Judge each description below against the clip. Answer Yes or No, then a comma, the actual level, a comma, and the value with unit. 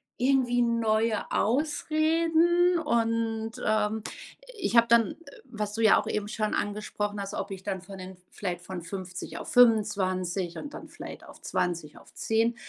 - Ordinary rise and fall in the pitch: Yes, average, 3.7 semitones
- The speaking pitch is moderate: No, high, 220 Hz